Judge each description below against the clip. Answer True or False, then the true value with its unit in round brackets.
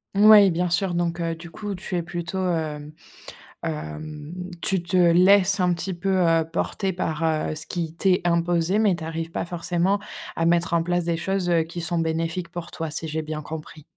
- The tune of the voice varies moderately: False (1.9 semitones)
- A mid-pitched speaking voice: True (170 Hz)